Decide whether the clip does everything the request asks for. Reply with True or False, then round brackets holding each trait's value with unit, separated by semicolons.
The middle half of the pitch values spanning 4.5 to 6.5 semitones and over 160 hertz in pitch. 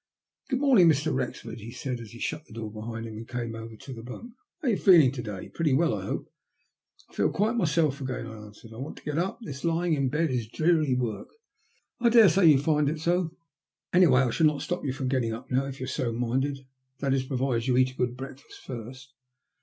False (5.2 semitones; 135 Hz)